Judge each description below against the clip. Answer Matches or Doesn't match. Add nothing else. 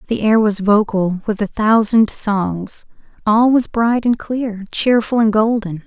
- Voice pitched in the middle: Doesn't match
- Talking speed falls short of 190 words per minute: Matches